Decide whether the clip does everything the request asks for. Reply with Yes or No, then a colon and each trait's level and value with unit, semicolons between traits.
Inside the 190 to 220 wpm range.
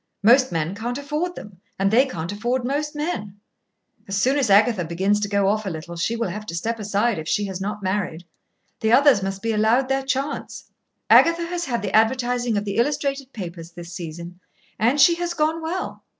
Yes: fast, 205 wpm